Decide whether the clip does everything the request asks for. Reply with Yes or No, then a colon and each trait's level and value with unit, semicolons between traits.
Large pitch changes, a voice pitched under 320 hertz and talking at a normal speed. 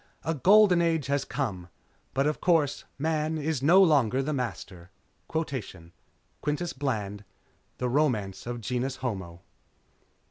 No: wide, 5.8 semitones; low, 135 Hz; slow, 120 wpm